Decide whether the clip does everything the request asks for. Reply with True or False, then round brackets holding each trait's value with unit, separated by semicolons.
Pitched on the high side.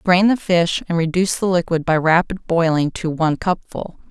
False (170 Hz)